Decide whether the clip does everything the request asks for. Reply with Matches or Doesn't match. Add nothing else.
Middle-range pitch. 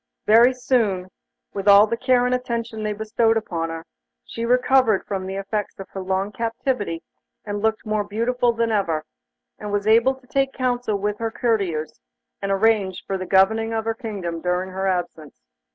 Doesn't match